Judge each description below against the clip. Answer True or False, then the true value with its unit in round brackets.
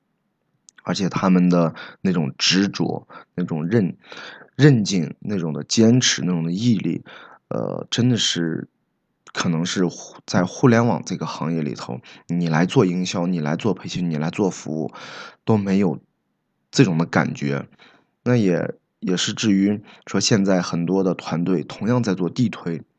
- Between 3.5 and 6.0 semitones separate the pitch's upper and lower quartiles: False (3.1 semitones)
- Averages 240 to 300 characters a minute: False (220 characters per minute)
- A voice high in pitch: False (90 Hz)